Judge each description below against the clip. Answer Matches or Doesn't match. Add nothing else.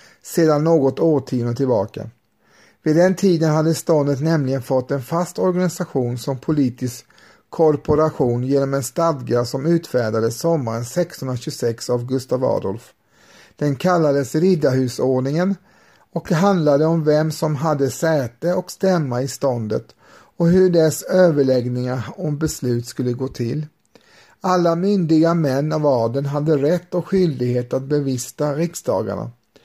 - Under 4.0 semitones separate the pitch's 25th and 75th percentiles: Doesn't match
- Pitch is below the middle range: Doesn't match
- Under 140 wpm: Matches